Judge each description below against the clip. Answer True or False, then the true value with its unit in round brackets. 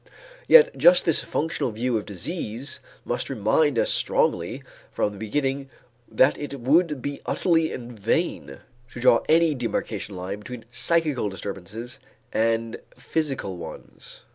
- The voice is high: False (125 Hz)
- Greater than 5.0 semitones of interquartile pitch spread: True (5.4 semitones)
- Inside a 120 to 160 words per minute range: True (135 wpm)